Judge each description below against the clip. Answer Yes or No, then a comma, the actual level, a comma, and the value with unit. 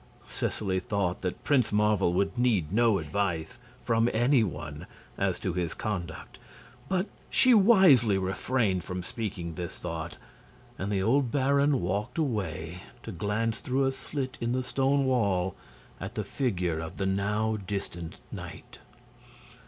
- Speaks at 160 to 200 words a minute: No, average, 145 wpm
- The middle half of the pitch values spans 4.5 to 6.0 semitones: Yes, wide, 5.6 semitones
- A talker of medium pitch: No, low, 105 Hz